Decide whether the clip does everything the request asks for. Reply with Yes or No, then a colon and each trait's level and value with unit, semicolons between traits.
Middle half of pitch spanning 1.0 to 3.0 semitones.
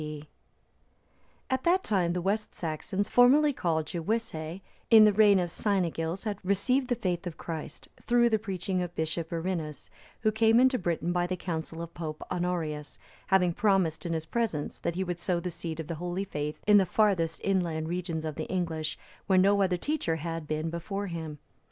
No: average, 3.7 semitones